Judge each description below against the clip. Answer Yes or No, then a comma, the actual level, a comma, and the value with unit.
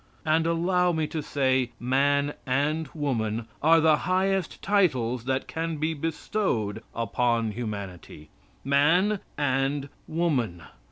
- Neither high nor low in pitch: Yes, medium, 145 Hz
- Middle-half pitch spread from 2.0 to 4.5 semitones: No, average, 5.0 semitones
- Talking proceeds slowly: Yes, slow, 115 wpm